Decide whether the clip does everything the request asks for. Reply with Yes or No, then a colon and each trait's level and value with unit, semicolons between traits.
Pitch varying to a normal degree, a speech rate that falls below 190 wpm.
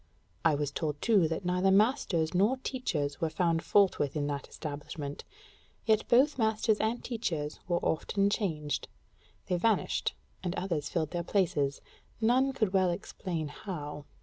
No: wide, 6.0 semitones; average, 150 wpm